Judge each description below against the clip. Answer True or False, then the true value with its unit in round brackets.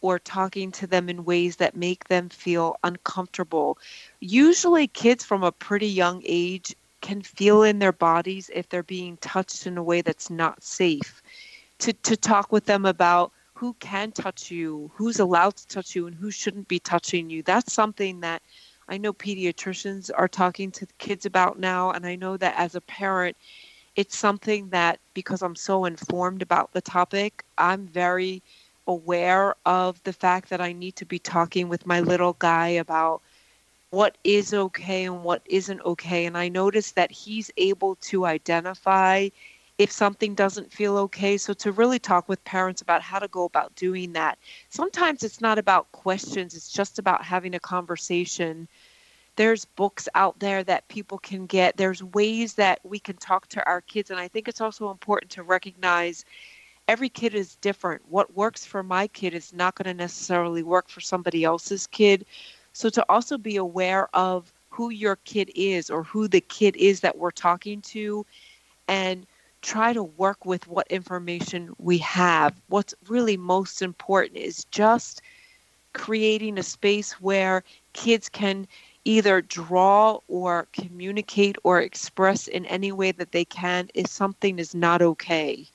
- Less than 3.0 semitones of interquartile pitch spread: True (2.5 semitones)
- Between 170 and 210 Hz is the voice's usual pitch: True (190 Hz)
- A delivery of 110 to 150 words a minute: False (170 wpm)